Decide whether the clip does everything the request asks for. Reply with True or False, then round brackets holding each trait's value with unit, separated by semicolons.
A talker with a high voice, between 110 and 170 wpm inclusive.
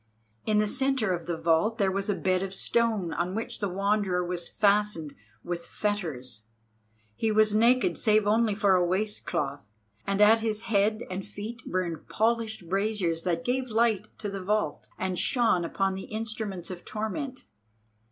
True (205 Hz; 165 wpm)